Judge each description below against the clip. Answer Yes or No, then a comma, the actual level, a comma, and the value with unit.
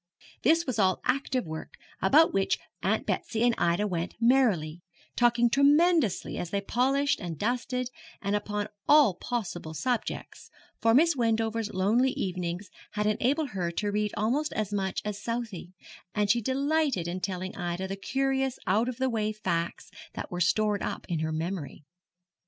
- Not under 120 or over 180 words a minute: Yes, average, 160 wpm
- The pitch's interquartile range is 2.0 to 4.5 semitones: No, average, 5.3 semitones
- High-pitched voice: Yes, high, 215 Hz